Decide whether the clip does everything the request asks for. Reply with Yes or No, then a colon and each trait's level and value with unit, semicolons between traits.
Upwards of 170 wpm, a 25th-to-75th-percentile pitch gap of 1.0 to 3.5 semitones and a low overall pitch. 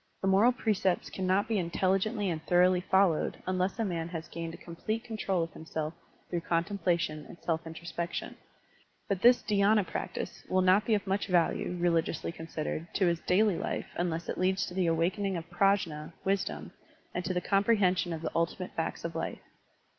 No: average, 180 wpm; average, 2.8 semitones; medium, 180 Hz